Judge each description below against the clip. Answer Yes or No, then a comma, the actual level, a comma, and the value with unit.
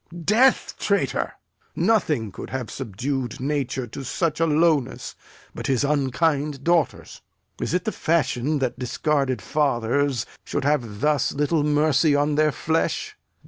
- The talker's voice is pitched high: No, medium, 145 Hz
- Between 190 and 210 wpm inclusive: No, slow, 135 wpm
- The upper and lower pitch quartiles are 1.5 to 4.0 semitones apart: Yes, average, 2.8 semitones